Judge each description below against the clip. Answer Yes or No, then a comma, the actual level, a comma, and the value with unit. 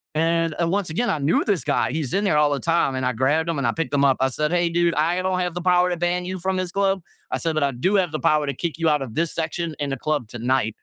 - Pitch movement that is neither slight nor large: Yes, average, 3.7 semitones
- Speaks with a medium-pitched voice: Yes, medium, 165 Hz